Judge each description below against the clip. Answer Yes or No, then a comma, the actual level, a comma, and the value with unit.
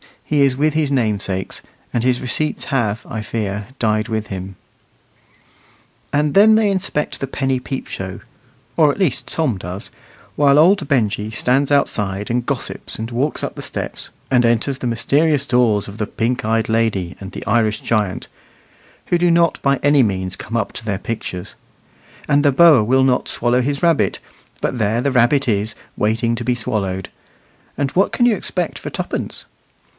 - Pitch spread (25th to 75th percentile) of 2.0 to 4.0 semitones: No, average, 4.9 semitones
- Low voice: Yes, low, 120 Hz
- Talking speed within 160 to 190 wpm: Yes, average, 175 wpm